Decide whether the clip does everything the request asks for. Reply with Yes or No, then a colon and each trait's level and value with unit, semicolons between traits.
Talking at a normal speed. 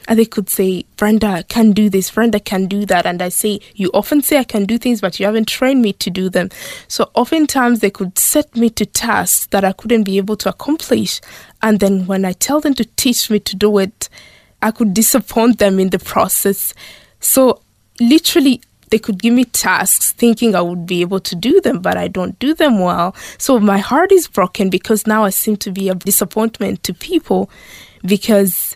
No: fast, 215 wpm